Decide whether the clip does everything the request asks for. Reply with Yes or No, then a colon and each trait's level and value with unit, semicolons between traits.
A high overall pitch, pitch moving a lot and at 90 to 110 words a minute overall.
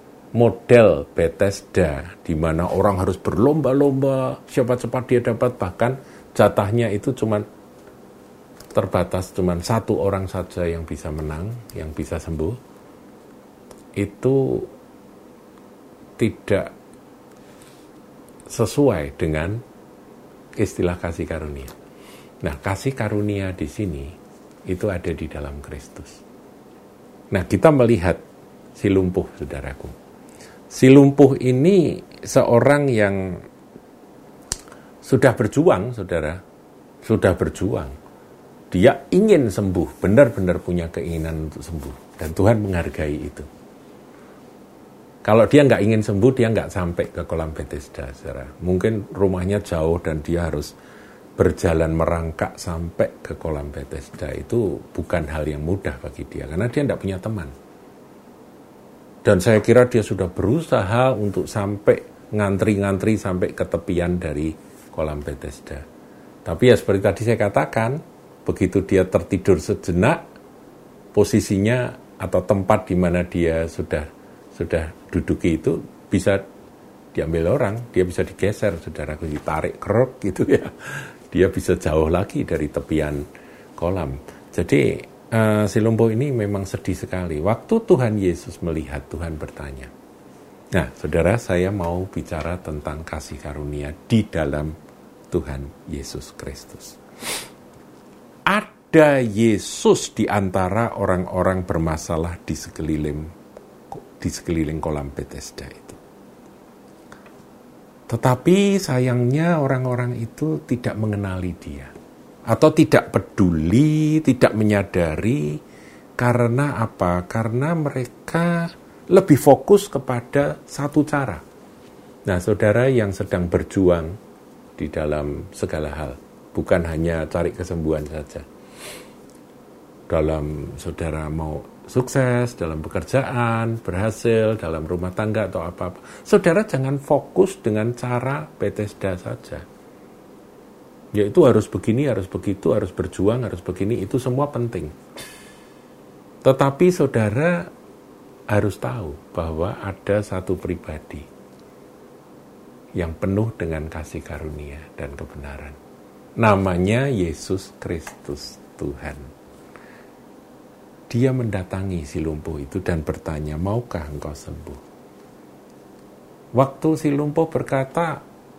No: very low, 95 Hz; wide, 6.5 semitones; average, 105 wpm